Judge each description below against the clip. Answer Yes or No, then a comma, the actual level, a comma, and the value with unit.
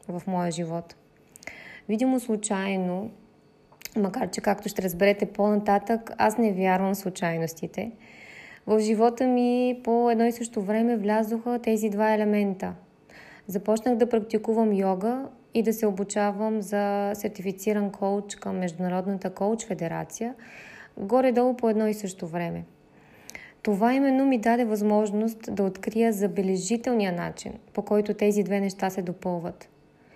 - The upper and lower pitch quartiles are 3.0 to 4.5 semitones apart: No, narrow, 2.6 semitones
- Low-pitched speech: No, high, 210 Hz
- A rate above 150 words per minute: No, average, 130 wpm